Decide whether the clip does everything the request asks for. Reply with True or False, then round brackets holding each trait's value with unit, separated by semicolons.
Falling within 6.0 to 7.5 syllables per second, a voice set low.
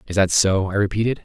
True (6.4 syllables/s; 100 Hz)